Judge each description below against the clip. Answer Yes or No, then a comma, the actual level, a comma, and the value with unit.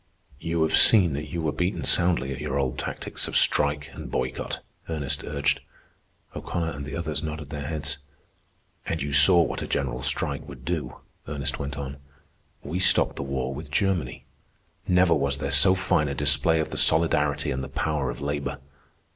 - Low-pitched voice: Yes, very low, 75 Hz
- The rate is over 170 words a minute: Yes, average, 180 wpm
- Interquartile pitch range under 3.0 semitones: Yes, narrow, 2.6 semitones